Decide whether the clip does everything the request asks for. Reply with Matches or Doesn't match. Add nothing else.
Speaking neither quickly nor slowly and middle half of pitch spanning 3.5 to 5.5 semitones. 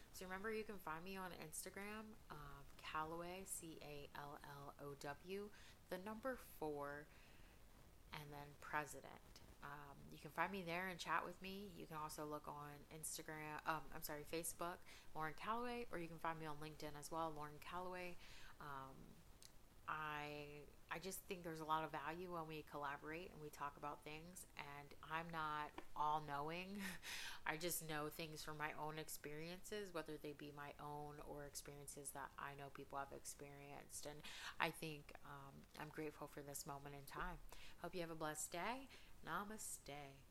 Doesn't match